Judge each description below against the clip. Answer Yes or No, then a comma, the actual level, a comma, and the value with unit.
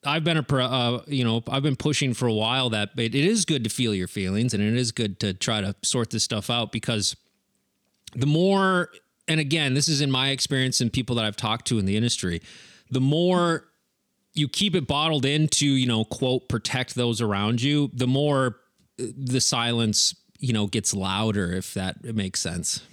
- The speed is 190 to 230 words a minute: Yes, fast, 205 wpm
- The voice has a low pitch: Yes, low, 125 Hz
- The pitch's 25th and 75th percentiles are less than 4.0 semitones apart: No, average, 4.3 semitones